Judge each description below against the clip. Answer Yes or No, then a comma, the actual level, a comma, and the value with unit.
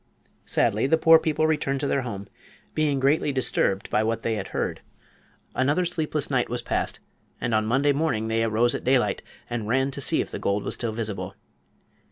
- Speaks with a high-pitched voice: No, low, 130 Hz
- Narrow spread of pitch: No, average, 4.5 semitones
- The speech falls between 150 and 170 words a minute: No, average, 195 wpm